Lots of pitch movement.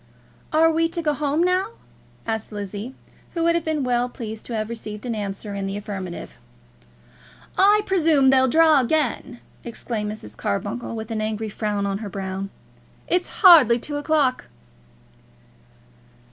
Yes: wide, 6.9 semitones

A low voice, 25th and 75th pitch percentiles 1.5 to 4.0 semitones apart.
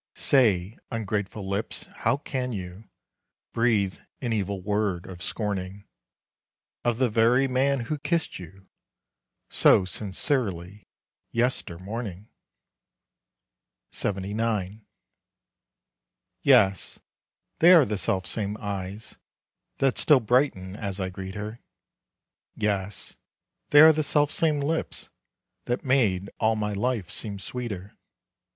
No: low, 105 Hz; average, 4.5 semitones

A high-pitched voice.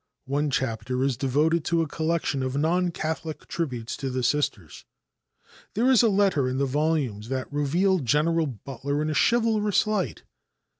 No: medium, 150 Hz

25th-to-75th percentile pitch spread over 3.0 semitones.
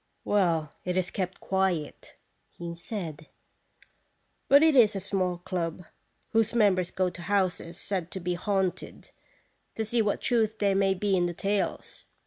No: average, 2.7 semitones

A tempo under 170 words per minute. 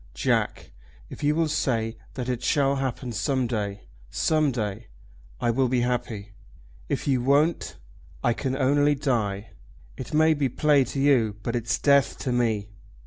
Yes: average, 160 wpm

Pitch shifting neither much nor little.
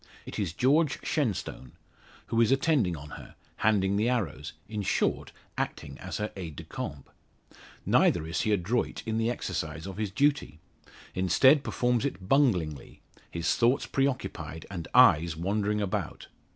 No: wide, 6.5 semitones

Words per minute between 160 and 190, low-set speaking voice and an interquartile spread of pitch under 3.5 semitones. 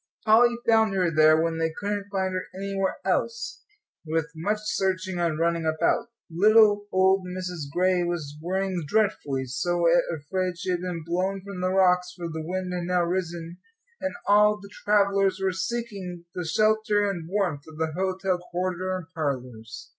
No: average, 165 wpm; medium, 185 Hz; average, 2.8 semitones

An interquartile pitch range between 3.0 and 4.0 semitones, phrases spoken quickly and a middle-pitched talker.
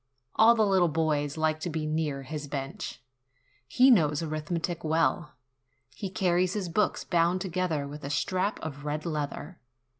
No: average, 3.5 semitones; average, 155 wpm; medium, 160 Hz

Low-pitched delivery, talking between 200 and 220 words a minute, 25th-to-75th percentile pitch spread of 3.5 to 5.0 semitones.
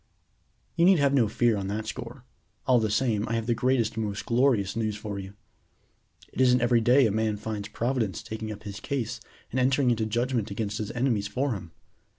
No: low, 115 Hz; fast, 205 wpm; average, 3.1 semitones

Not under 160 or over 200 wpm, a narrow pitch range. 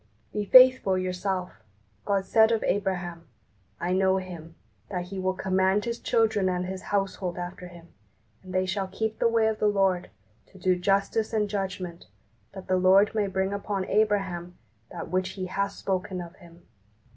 Yes: average, 170 wpm; narrow, 1.9 semitones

